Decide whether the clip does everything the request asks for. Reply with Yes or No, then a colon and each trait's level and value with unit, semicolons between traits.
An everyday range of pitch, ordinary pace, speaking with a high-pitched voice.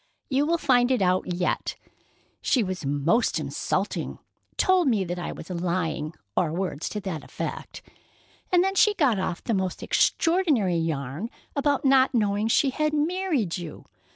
No: wide, 8.4 semitones; average, 150 wpm; high, 210 Hz